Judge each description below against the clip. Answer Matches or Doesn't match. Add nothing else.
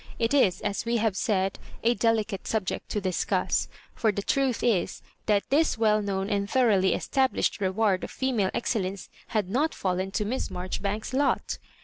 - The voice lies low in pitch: Doesn't match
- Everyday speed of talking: Matches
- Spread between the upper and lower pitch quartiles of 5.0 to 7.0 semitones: Doesn't match